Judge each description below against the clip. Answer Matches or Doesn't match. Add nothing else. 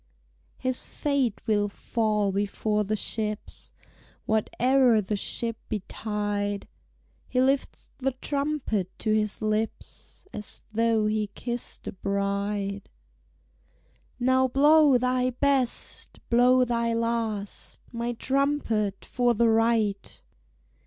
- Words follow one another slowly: Matches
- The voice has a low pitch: Doesn't match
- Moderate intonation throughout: Matches